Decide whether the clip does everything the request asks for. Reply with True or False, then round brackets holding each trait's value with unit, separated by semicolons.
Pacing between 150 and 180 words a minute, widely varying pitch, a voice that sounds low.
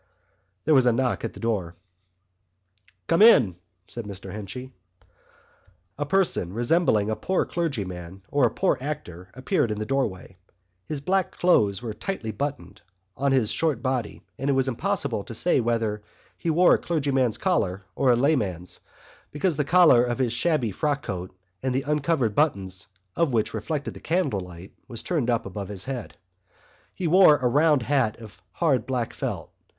True (165 wpm; 6.0 semitones; 125 Hz)